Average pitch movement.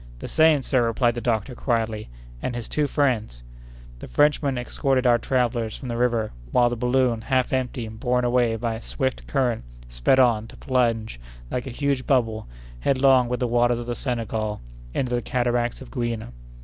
No: narrow, 2.1 semitones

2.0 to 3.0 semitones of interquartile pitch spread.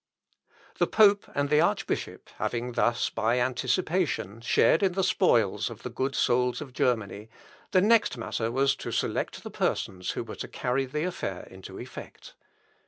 No: average, 5.3 semitones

